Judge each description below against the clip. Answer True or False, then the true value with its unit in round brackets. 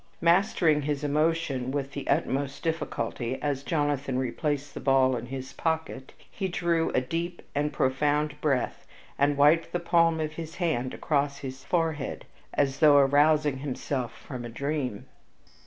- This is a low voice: False (145 Hz)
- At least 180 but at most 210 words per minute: False (150 wpm)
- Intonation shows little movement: False (3.1 semitones)